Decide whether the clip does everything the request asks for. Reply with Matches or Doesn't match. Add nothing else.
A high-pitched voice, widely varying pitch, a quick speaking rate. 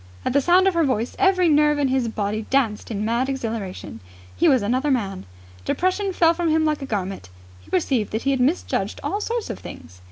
Matches